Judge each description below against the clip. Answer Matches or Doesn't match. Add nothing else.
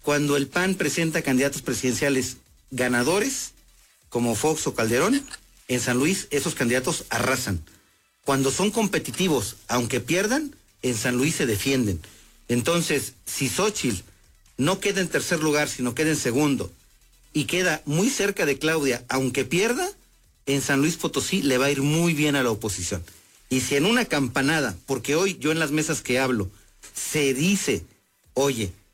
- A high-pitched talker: Doesn't match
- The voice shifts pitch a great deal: Doesn't match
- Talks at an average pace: Matches